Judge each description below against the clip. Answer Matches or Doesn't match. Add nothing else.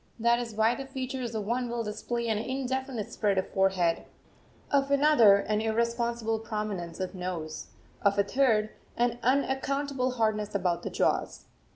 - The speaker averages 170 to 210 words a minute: Doesn't match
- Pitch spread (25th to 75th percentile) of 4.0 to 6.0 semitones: Doesn't match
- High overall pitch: Matches